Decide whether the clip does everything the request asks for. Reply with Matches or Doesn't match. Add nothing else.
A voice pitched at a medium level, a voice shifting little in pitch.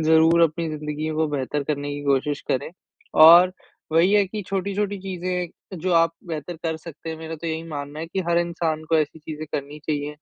Matches